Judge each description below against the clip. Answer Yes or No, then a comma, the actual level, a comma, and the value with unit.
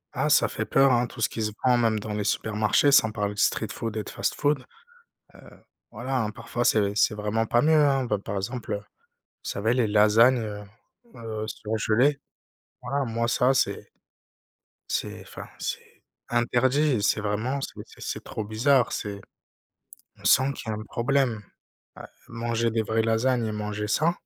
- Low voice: Yes, low, 115 Hz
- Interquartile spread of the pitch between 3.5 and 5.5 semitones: No, average, 3.0 semitones